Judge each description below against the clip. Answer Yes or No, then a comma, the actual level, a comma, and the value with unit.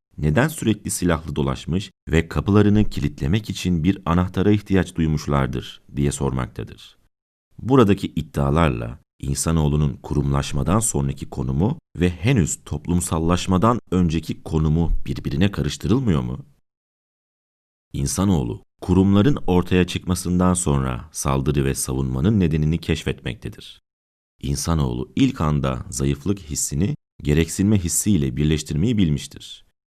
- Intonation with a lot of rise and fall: No, average, 4.8 semitones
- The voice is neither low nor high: No, very low, 80 Hz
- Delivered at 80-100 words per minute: Yes, slow, 95 wpm